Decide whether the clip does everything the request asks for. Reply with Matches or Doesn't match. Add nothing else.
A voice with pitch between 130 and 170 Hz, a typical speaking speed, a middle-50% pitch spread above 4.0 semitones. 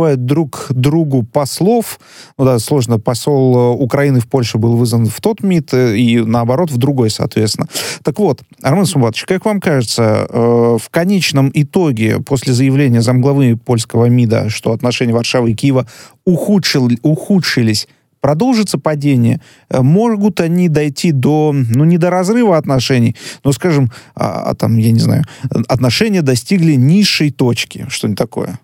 Matches